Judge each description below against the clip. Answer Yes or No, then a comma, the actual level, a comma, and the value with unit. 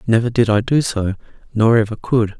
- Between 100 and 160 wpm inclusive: No, average, 200 wpm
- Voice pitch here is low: Yes, low, 115 Hz